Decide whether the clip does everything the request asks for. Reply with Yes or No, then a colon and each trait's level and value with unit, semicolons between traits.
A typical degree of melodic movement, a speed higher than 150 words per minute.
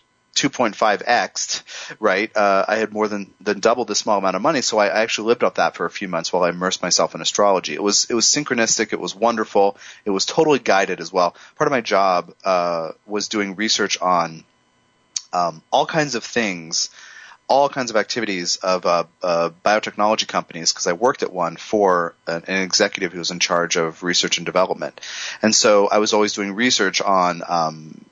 Yes: average, 3.5 semitones; fast, 205 wpm